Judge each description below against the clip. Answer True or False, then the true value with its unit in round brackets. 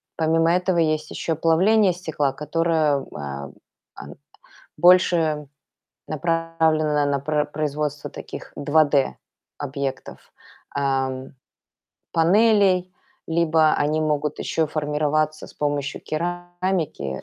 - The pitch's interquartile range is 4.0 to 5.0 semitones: False (2.4 semitones)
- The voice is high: False (155 Hz)